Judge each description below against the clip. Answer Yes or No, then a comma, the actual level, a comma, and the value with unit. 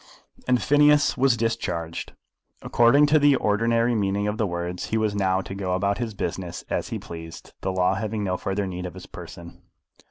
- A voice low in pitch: Yes, low, 100 Hz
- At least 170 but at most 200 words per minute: Yes, average, 190 wpm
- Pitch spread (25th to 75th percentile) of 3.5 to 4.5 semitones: Yes, average, 4.2 semitones